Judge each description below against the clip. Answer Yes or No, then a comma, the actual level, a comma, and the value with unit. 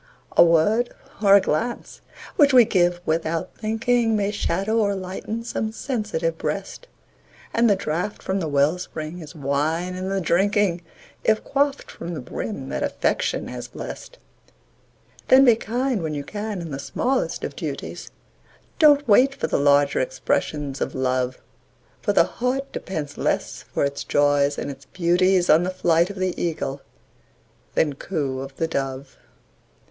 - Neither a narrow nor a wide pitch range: No, wide, 6.6 semitones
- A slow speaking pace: No, average, 160 wpm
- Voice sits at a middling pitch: Yes, medium, 180 Hz